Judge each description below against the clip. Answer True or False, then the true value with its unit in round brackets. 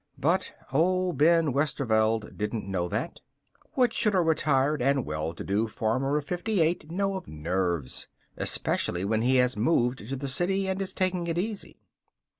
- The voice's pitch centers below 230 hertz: True (140 Hz)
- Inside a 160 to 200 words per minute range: True (170 wpm)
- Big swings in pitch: True (8.3 semitones)